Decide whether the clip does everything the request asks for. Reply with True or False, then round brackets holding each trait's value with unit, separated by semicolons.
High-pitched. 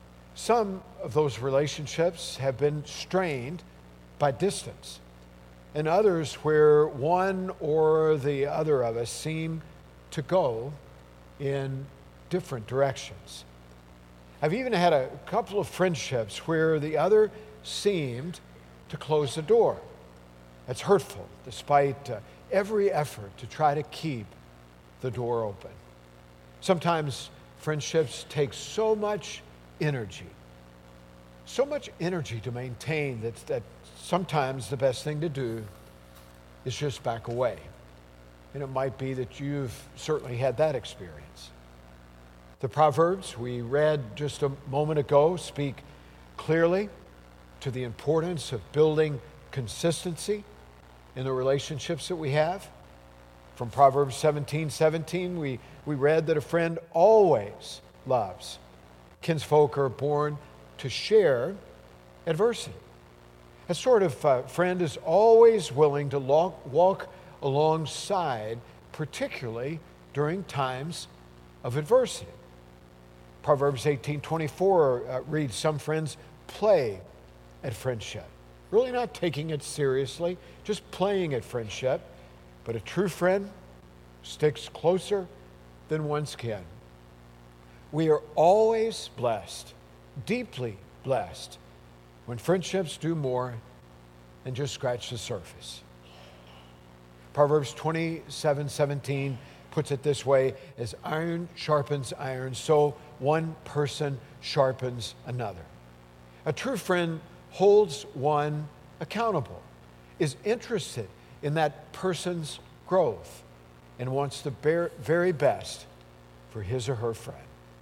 False (140 Hz)